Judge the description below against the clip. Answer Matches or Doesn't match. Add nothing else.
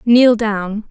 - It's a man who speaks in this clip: Doesn't match